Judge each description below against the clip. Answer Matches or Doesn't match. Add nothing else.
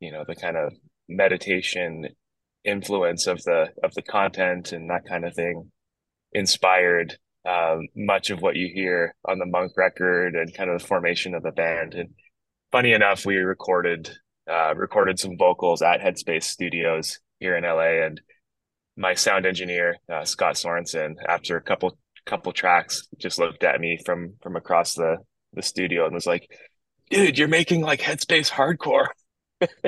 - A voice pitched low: Matches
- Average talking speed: Matches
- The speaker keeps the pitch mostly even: Matches